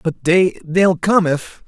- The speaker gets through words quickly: No, slow, 110 wpm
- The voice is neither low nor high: Yes, medium, 175 Hz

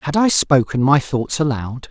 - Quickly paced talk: No, average, 190 wpm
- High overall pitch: No, low, 135 Hz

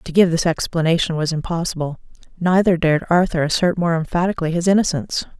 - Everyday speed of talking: Yes, average, 155 wpm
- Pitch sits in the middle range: Yes, medium, 170 Hz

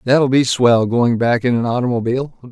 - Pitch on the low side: Yes, low, 125 Hz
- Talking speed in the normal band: Yes, average, 190 wpm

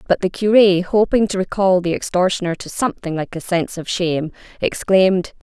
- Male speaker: No, female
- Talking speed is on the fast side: No, average, 175 wpm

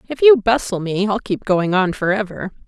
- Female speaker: Yes, female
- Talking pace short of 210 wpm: No, fast, 225 wpm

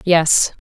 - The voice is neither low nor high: Yes, medium, 165 Hz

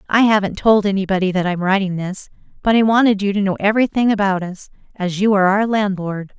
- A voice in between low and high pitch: No, high, 200 Hz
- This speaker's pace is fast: Yes, fast, 215 wpm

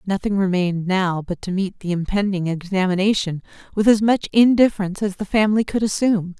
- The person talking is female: Yes, female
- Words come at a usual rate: Yes, average, 170 wpm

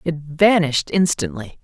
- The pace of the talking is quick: No, slow, 110 wpm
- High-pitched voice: No, medium, 165 Hz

